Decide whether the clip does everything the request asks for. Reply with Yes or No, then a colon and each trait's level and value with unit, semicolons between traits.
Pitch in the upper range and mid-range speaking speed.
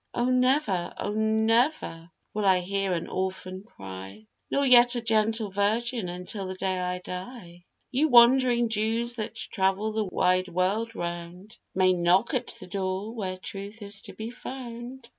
Yes: high, 205 Hz; average, 160 wpm